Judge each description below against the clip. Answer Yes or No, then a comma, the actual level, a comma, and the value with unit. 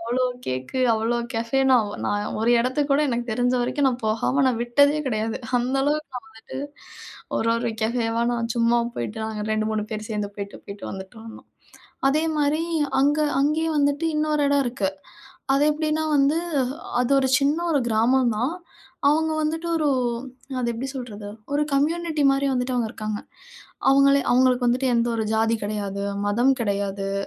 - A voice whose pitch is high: Yes, high, 245 Hz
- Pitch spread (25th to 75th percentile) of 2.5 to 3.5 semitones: No, average, 4.3 semitones